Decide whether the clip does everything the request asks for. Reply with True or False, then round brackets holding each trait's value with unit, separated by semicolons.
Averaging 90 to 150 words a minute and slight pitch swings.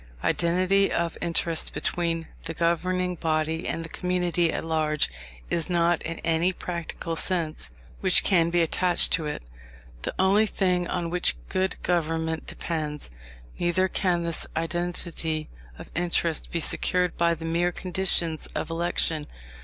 True (140 wpm; 1.5 semitones)